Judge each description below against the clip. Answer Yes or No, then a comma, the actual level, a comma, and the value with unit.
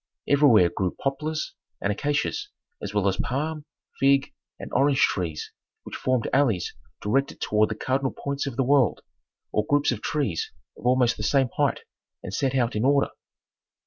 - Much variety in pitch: No, average, 4.7 semitones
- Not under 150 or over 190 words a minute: Yes, average, 165 wpm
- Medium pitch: No, low, 130 Hz